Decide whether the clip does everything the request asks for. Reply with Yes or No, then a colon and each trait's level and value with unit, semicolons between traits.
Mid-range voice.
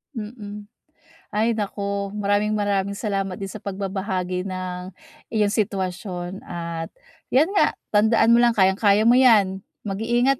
No: high, 200 Hz